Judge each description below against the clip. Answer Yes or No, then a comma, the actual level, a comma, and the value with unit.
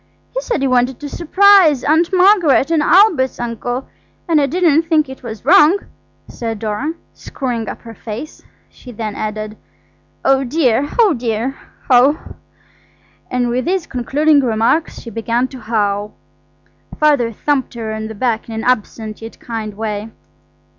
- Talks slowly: No, average, 155 wpm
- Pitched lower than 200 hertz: No, very high, 250 Hz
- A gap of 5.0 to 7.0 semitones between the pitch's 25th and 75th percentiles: Yes, average, 5.3 semitones